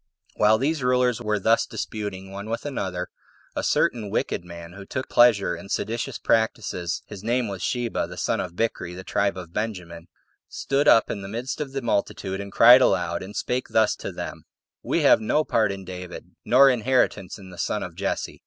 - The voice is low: Yes, low, 105 Hz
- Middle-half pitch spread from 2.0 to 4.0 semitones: No, average, 4.4 semitones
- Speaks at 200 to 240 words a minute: Yes, fast, 205 wpm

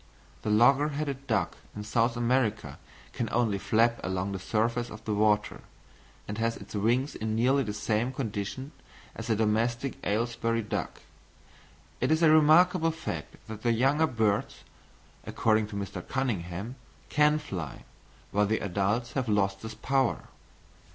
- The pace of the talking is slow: No, average, 150 wpm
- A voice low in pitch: Yes, low, 115 Hz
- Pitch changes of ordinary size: Yes, average, 3.9 semitones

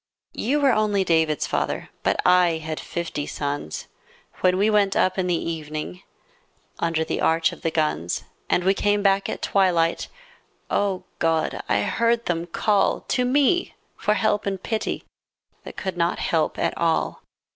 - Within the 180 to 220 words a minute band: No, average, 165 wpm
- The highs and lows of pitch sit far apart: No, average, 4.1 semitones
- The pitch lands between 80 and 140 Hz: No, medium, 180 Hz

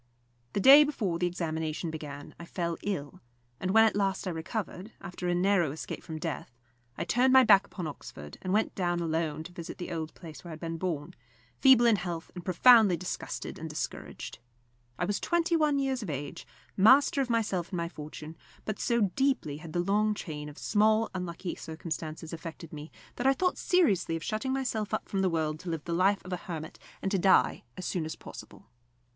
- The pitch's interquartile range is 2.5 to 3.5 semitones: No, average, 4.9 semitones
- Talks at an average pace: No, fast, 210 wpm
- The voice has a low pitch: No, medium, 180 Hz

